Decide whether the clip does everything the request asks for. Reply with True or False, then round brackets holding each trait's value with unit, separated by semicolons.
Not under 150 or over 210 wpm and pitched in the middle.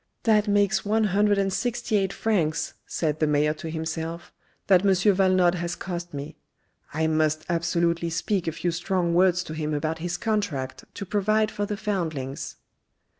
True (175 wpm; 175 Hz)